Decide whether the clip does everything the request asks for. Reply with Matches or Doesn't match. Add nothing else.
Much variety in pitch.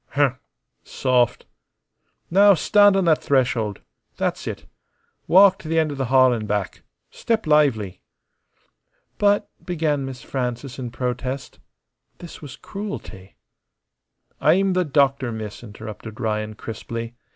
Matches